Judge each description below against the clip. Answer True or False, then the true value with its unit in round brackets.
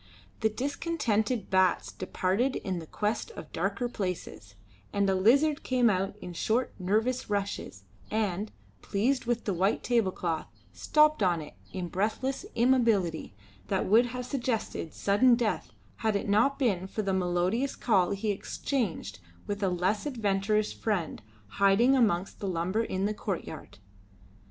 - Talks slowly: False (145 wpm)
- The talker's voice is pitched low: False (205 Hz)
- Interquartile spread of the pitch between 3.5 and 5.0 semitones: True (4.4 semitones)